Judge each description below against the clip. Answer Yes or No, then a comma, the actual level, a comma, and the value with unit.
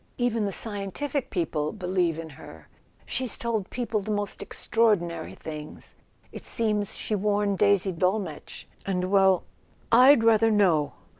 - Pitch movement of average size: Yes, average, 3.8 semitones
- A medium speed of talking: No, slow, 130 wpm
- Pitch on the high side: Yes, high, 200 Hz